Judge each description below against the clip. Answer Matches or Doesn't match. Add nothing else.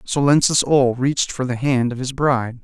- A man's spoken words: Matches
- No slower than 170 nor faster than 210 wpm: Matches